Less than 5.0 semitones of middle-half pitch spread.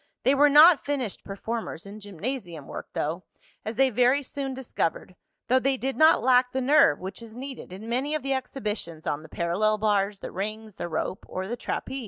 No: average, 5.3 semitones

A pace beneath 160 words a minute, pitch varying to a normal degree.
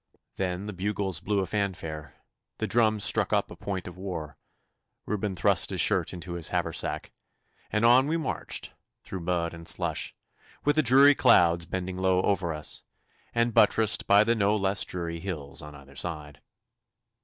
No: average, 165 wpm; average, 3.9 semitones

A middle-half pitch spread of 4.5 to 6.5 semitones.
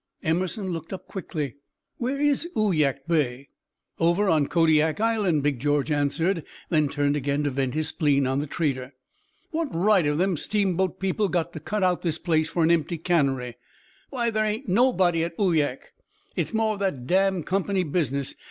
Yes: average, 4.8 semitones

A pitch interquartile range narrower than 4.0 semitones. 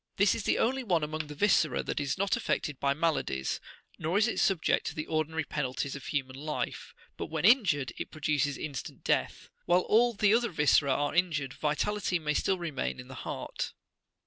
No: average, 5.1 semitones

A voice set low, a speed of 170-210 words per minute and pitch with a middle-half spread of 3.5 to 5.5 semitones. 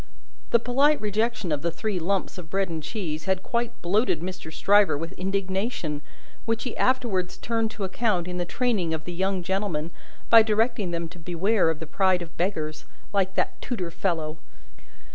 No: high, 190 Hz; average, 180 wpm; average, 4.3 semitones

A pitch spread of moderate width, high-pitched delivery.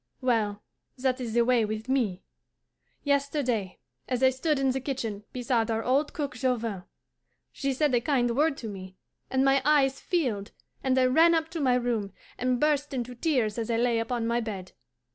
Yes: average, 3.2 semitones; very high, 250 Hz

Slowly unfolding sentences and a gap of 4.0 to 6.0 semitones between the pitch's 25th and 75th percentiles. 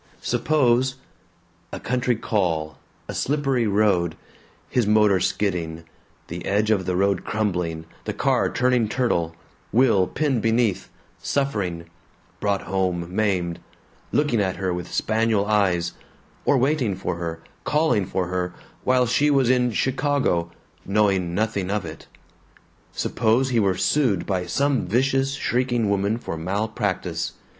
Yes: slow, 130 wpm; average, 5.3 semitones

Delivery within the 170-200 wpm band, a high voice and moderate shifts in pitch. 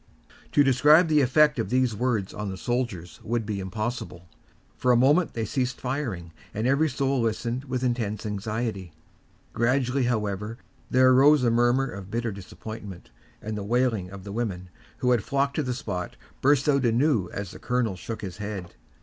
No: average, 175 wpm; low, 120 Hz; average, 4.0 semitones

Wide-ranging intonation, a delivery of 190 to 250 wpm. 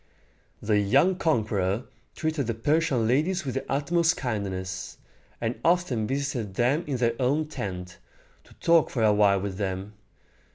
No: wide, 6.6 semitones; average, 150 wpm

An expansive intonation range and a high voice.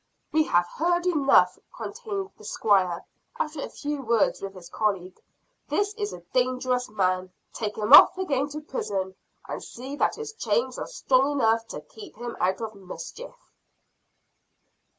Yes: wide, 7.9 semitones; very high, 255 Hz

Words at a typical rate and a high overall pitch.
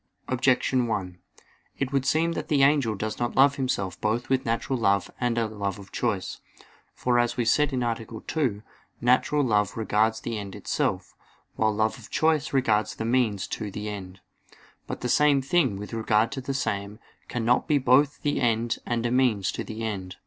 No: average, 185 wpm; low, 115 Hz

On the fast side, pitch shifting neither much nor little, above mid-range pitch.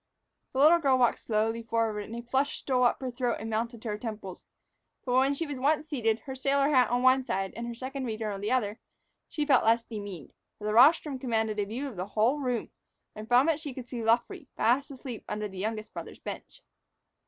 Yes: fast, 225 wpm; average, 3.4 semitones; high, 240 Hz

